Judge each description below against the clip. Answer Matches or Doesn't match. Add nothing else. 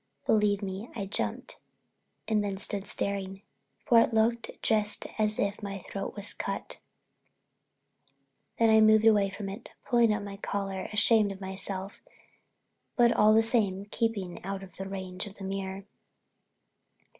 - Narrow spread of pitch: Matches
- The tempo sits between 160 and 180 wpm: Doesn't match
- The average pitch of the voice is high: Matches